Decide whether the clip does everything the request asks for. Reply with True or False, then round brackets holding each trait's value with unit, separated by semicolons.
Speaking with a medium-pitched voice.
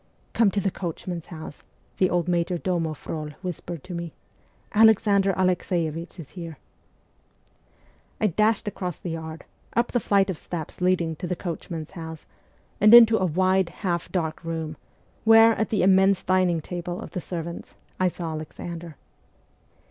True (175 Hz)